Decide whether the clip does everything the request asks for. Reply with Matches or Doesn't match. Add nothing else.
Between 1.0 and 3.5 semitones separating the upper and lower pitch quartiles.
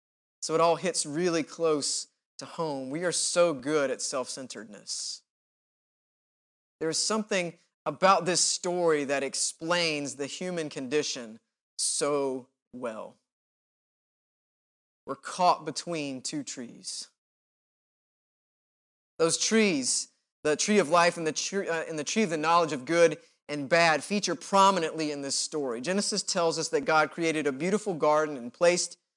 Matches